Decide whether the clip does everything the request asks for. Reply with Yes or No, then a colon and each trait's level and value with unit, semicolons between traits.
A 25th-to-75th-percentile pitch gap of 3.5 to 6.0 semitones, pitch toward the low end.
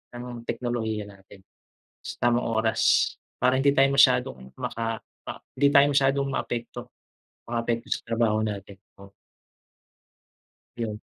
No: average, 2.9 semitones; low, 115 Hz